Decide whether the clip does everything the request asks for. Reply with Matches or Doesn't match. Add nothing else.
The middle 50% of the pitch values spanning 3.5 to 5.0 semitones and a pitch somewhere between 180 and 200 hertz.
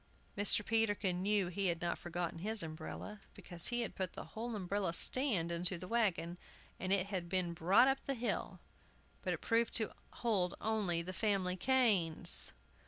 Matches